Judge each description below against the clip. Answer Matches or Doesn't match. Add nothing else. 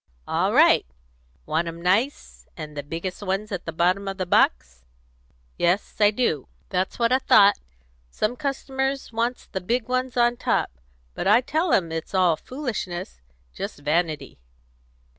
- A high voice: Matches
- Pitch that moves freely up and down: Matches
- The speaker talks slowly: Doesn't match